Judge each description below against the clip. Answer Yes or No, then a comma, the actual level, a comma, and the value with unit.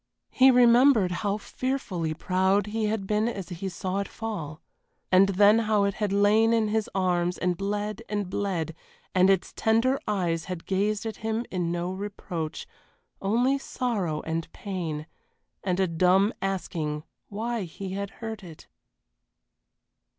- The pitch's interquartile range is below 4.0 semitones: Yes, average, 3.4 semitones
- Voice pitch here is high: Yes, high, 195 Hz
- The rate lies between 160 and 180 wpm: No, average, 150 wpm